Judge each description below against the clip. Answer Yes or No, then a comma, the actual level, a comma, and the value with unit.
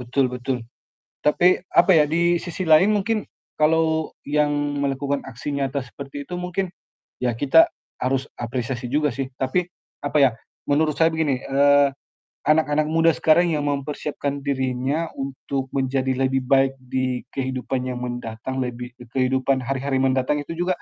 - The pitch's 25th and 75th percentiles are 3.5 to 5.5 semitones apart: No, average, 2.8 semitones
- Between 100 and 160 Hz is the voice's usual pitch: Yes, medium, 140 Hz